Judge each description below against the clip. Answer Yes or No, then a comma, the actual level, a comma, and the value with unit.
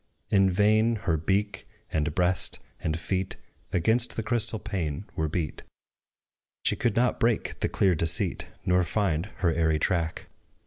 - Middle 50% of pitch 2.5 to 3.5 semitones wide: No, average, 4.4 semitones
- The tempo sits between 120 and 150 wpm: Yes, average, 145 wpm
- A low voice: Yes, very low, 95 Hz